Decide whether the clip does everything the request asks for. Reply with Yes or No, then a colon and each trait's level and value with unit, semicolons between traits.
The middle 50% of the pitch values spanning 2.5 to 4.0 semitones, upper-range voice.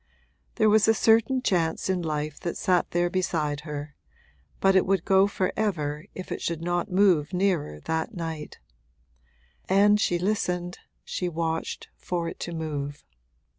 No: average, 3.2 semitones; medium, 175 Hz